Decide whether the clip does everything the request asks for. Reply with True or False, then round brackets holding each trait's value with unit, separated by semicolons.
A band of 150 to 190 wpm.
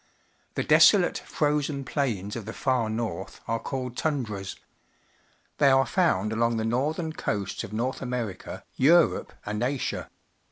False (135 wpm)